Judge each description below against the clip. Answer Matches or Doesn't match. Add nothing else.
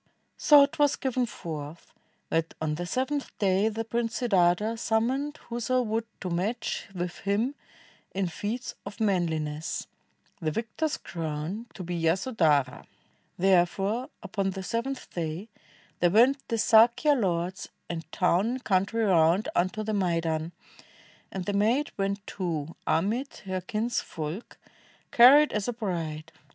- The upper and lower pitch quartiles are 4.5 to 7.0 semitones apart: Matches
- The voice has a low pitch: Doesn't match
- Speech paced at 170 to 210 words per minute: Doesn't match